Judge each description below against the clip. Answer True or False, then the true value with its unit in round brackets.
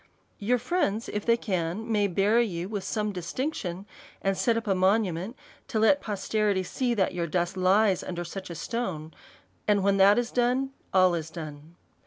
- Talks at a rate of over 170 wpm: True (180 wpm)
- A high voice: True (200 Hz)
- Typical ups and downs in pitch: True (4.0 semitones)